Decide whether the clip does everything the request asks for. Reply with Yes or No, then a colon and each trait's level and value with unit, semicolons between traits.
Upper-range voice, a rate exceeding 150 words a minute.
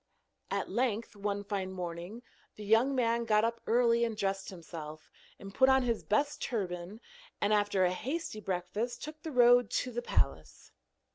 Yes: high, 215 Hz; average, 165 wpm